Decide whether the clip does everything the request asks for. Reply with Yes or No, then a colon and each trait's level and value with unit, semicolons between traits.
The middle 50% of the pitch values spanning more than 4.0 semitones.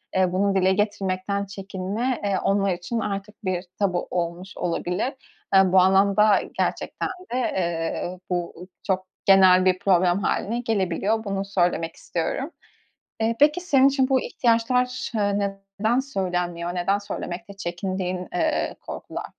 No: average, 3.0 semitones